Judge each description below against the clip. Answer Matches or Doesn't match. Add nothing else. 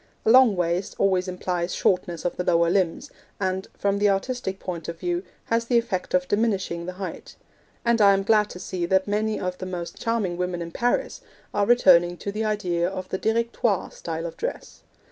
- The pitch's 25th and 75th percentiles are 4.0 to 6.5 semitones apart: Doesn't match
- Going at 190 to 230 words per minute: Matches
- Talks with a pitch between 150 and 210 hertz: Matches